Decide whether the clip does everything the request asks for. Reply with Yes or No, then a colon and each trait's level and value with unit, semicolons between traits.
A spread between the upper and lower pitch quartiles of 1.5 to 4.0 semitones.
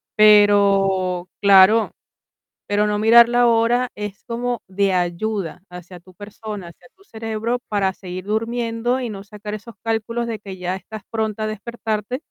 Yes: average, 2.7 semitones